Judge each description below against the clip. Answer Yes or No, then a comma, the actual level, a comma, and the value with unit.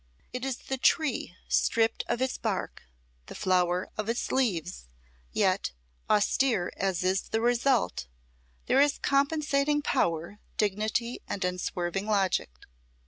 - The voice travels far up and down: Yes, wide, 6.2 semitones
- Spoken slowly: Yes, slow, 125 wpm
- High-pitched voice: Yes, high, 220 Hz